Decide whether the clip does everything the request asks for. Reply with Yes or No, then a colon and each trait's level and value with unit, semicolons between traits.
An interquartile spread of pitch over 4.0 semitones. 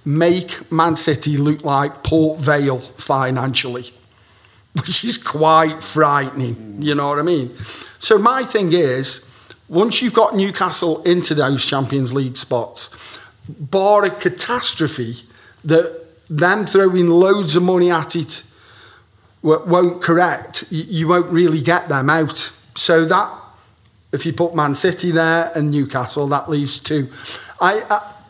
Yes: average, 4.7 semitones